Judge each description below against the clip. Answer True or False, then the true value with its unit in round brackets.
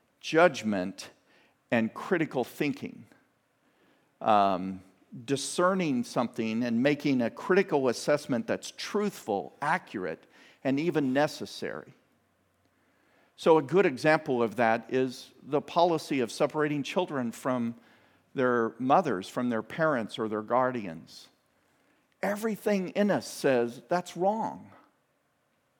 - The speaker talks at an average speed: False (105 wpm)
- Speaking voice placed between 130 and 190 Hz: True (140 Hz)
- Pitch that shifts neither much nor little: False (6.9 semitones)